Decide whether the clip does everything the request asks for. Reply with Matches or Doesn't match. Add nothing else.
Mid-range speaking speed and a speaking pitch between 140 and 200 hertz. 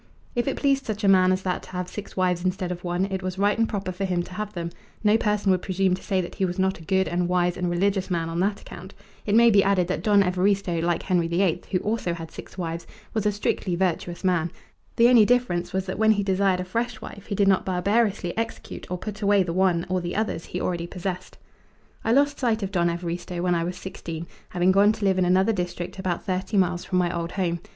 Doesn't match